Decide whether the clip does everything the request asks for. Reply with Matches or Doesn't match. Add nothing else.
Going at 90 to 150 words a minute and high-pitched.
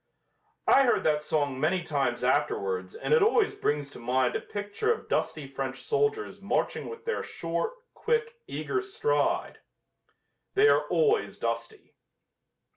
Matches